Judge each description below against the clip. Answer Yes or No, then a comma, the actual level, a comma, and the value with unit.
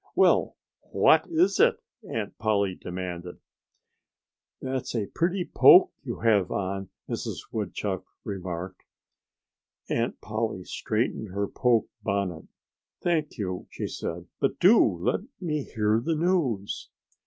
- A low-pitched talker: Yes, low, 105 Hz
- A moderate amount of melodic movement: No, wide, 7.0 semitones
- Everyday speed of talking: No, slow, 120 wpm